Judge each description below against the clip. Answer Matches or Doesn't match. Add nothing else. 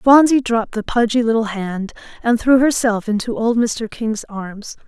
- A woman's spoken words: Matches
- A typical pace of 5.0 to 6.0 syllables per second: Doesn't match